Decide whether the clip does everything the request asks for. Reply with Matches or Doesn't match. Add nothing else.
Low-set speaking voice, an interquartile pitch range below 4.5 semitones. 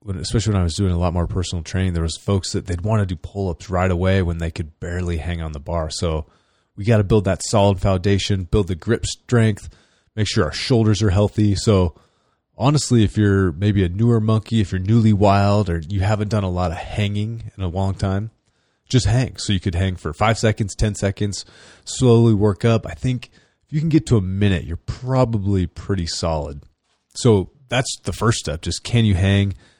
Matches